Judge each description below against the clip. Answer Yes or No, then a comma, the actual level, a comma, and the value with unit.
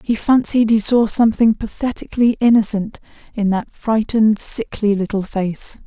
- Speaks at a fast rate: No, slow, 135 wpm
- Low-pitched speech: No, high, 220 Hz